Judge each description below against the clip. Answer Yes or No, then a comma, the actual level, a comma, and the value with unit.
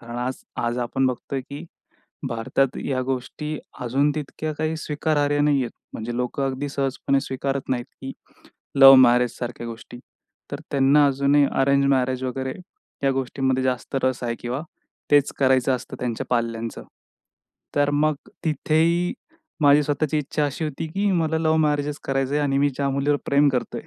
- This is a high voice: No, low, 135 Hz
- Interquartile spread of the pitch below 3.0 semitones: Yes, narrow, 2.4 semitones